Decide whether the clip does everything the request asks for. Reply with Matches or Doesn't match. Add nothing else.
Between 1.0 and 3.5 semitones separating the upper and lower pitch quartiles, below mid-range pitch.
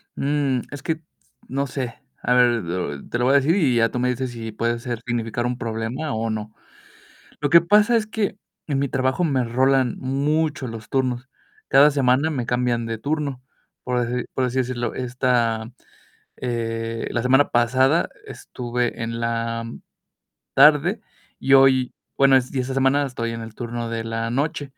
Matches